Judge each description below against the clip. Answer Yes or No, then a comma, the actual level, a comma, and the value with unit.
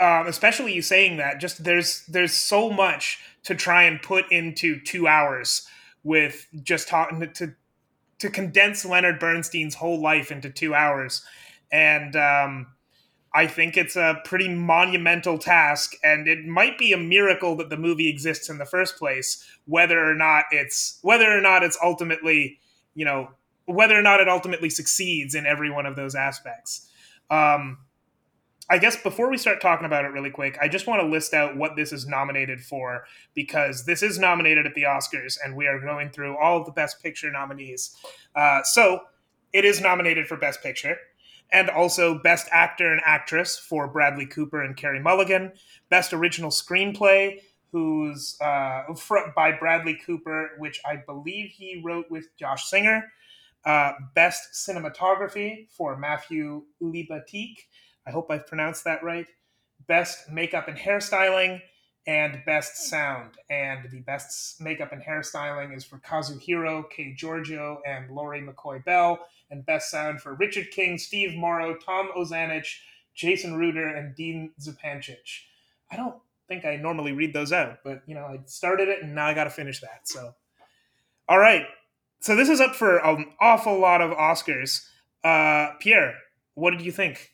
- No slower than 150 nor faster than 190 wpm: Yes, average, 165 wpm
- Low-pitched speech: No, medium, 160 Hz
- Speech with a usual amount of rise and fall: Yes, average, 3.4 semitones